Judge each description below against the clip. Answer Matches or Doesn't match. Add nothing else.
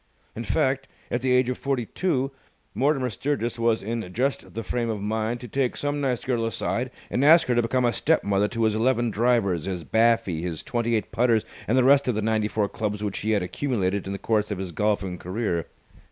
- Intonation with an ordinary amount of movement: Matches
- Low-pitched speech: Matches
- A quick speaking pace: Matches